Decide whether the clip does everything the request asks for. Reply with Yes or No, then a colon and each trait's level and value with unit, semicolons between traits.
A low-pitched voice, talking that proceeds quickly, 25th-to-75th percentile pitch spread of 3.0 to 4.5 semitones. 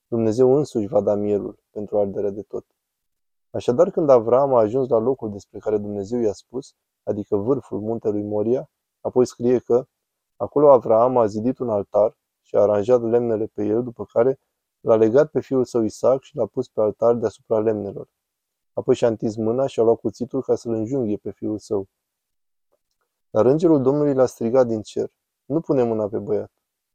Yes: low, 115 Hz; fast, 180 wpm; average, 3.5 semitones